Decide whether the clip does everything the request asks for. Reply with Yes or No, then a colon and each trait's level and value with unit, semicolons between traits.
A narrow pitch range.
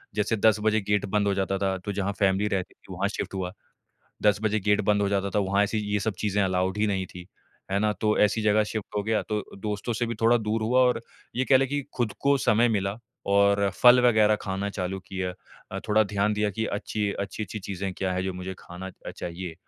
Yes: narrow, 2.0 semitones